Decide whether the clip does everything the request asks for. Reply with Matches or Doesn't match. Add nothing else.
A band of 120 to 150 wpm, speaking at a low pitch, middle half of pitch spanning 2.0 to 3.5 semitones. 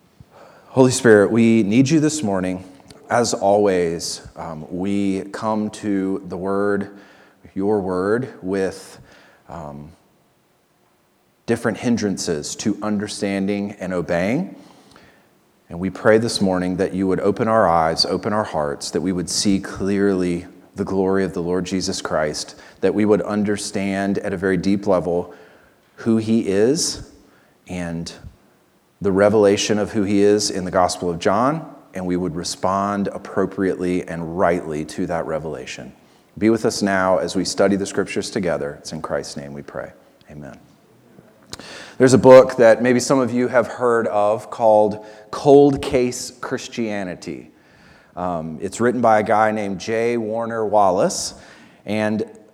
Matches